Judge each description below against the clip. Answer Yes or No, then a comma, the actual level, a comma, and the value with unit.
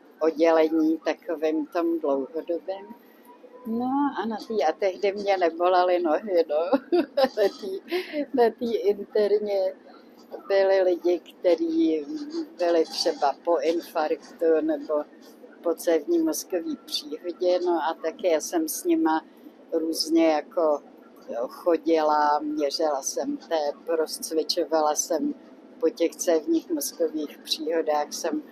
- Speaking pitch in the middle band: Yes, medium, 175 Hz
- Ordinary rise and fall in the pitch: No, wide, 8.7 semitones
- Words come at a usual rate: No, slow, 110 wpm